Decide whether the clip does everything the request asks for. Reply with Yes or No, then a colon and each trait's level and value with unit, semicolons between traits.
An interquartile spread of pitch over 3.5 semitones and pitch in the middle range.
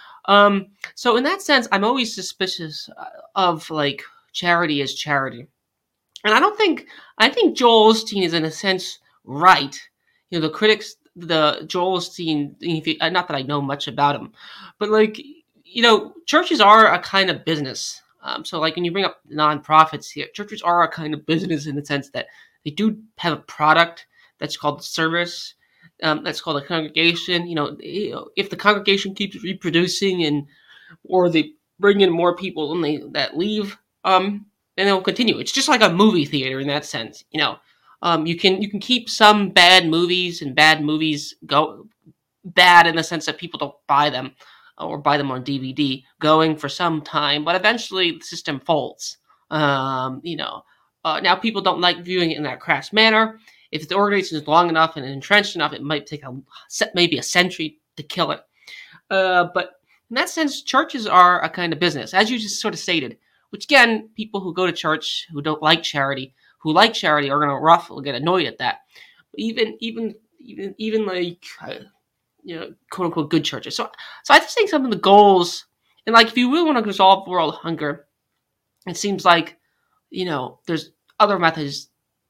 Yes: average, 5.1 semitones; medium, 175 Hz